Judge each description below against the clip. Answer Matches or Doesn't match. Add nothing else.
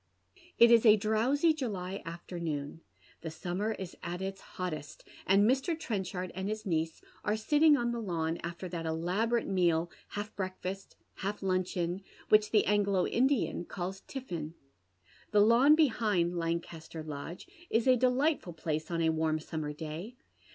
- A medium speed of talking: Matches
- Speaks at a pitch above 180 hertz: Matches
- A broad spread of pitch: Doesn't match